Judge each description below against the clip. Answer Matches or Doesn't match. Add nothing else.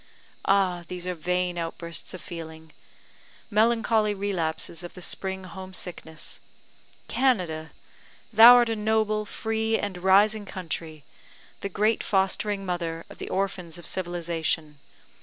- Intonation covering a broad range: Doesn't match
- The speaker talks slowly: Matches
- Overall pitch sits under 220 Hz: Matches